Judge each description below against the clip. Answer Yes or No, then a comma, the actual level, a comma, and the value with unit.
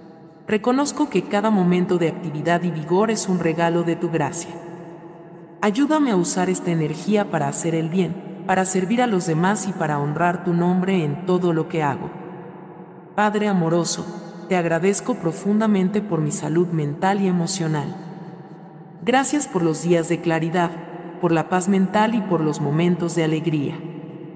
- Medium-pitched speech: Yes, medium, 175 Hz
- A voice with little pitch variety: Yes, narrow, 2.3 semitones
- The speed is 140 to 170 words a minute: Yes, average, 160 wpm